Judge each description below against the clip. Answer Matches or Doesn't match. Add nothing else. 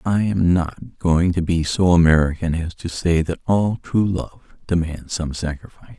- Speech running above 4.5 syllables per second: Doesn't match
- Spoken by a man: Matches